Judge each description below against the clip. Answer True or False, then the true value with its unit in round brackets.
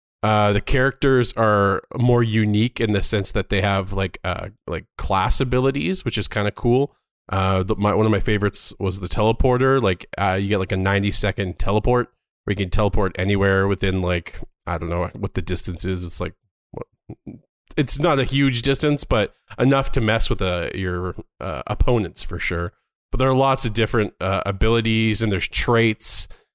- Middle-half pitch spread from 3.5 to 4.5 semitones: True (3.8 semitones)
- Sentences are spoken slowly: False (190 wpm)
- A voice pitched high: False (105 Hz)